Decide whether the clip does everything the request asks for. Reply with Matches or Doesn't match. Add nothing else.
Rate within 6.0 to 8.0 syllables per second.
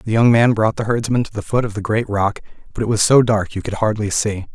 Doesn't match